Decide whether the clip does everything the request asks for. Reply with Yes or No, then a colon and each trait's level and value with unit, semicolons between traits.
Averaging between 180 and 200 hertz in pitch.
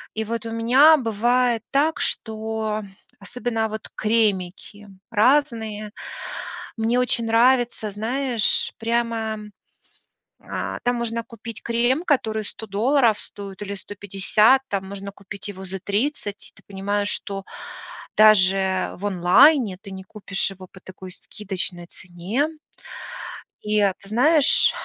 No: high, 215 Hz